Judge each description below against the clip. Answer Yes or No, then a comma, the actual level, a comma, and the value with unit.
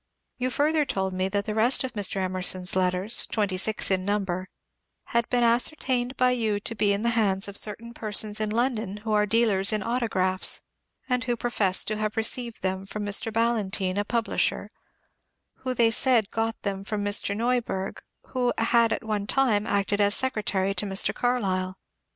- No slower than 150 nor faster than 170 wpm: No, average, 185 wpm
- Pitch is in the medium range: No, high, 215 Hz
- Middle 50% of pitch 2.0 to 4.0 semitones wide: Yes, average, 3.2 semitones